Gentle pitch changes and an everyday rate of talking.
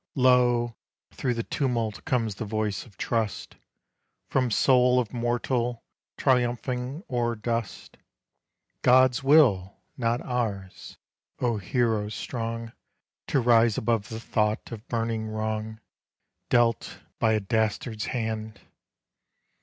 No: narrow, 2.1 semitones; slow, 110 wpm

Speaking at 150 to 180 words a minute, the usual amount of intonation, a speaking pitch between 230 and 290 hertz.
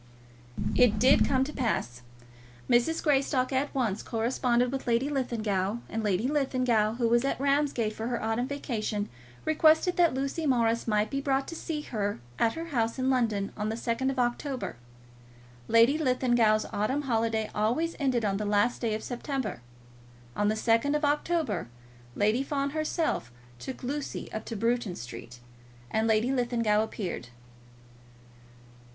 Yes: average, 155 wpm; average, 3.9 semitones; high, 240 Hz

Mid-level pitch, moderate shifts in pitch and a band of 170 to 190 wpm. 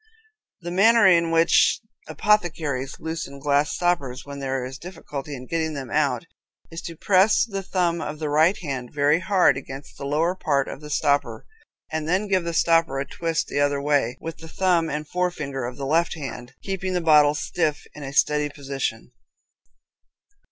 Yes: medium, 155 Hz; average, 3.6 semitones; average, 180 wpm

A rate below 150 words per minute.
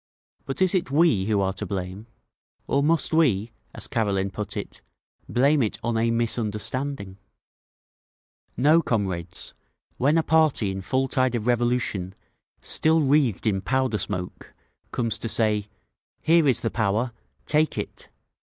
Yes: average, 140 wpm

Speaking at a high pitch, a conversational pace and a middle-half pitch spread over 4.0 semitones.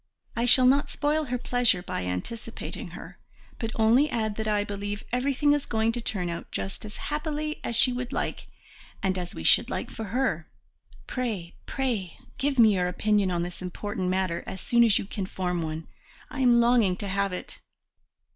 Yes: high, 220 Hz; average, 190 wpm; average, 5.1 semitones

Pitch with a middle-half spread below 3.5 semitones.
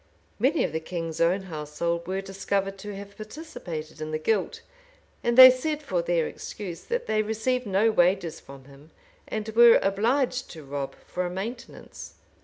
No: average, 5.3 semitones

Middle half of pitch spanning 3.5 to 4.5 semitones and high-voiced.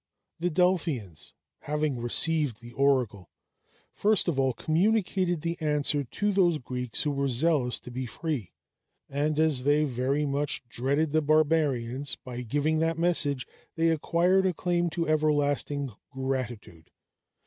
No: average, 4.0 semitones; medium, 145 Hz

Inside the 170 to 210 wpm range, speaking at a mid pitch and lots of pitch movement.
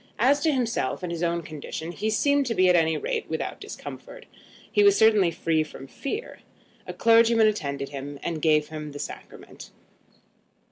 Yes: average, 175 wpm; medium, 180 Hz; wide, 7.1 semitones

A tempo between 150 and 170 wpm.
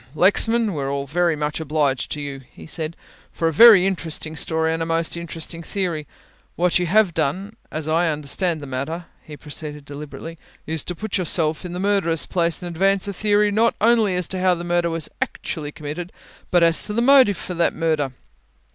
No: average, 200 wpm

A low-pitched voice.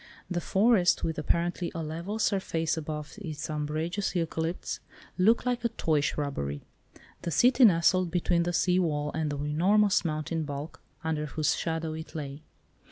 No: medium, 165 Hz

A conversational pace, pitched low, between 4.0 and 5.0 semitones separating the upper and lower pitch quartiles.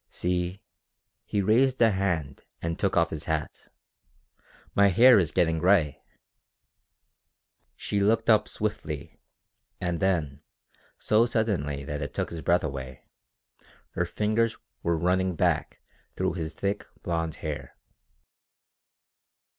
No: slow, 120 wpm; very low, 90 Hz; average, 4.5 semitones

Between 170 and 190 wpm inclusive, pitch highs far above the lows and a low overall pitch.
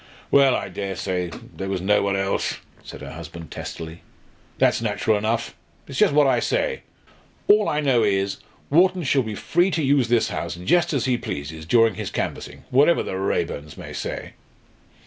Yes: average, 180 wpm; wide, 6.8 semitones; low, 110 Hz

